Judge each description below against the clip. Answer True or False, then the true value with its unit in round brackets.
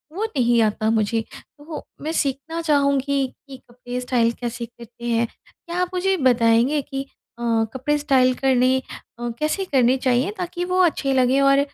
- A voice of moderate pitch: False (265 Hz)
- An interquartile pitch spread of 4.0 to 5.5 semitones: False (3.5 semitones)